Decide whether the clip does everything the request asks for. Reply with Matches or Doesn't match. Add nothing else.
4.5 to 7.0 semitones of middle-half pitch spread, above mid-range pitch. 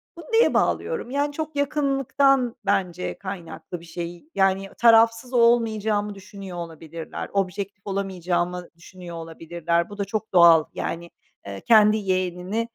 Matches